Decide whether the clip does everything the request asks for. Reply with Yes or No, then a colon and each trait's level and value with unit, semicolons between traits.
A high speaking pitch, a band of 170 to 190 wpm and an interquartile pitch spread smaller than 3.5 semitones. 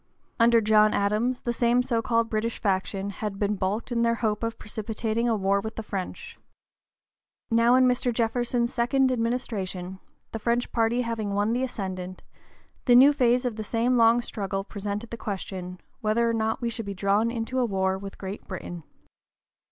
Yes: high, 225 Hz; average, 180 wpm; average, 2.9 semitones